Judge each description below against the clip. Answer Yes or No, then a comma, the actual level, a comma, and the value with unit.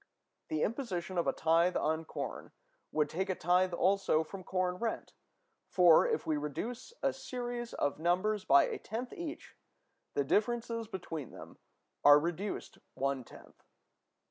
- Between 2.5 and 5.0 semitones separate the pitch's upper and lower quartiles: No, wide, 5.5 semitones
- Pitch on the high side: No, medium, 180 Hz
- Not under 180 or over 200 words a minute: No, average, 145 wpm